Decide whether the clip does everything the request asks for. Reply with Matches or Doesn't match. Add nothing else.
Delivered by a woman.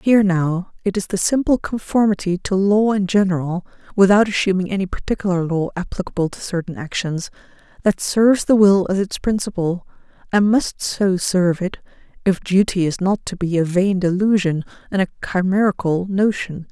Matches